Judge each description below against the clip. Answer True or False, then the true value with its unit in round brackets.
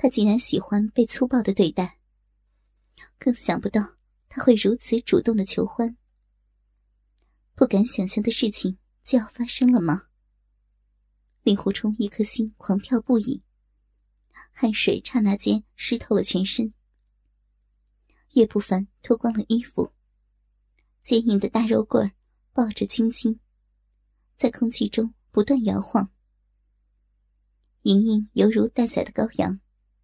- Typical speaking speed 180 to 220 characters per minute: True (185 characters per minute)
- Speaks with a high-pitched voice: True (215 Hz)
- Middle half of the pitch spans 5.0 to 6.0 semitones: False (4.5 semitones)